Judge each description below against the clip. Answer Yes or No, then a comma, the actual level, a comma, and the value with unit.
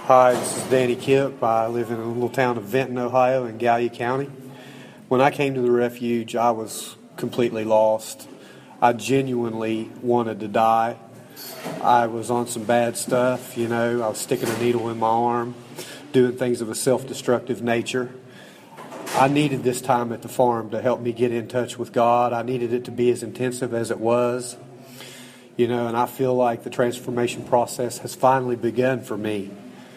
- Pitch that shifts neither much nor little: No, narrow, 1.3 semitones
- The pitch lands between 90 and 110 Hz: No, low, 120 Hz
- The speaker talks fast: No, average, 190 wpm